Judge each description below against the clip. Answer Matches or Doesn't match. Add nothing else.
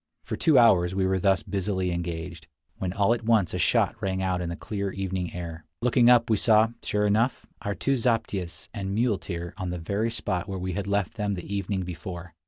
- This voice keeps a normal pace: Doesn't match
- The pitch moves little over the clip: Doesn't match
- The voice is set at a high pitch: Doesn't match